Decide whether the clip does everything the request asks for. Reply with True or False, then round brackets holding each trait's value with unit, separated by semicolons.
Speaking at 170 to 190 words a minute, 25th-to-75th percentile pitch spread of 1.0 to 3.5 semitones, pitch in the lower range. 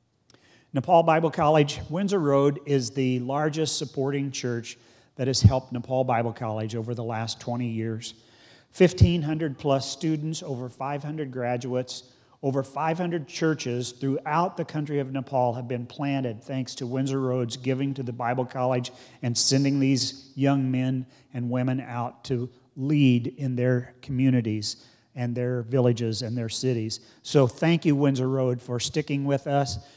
False (150 wpm; 2.5 semitones; 130 Hz)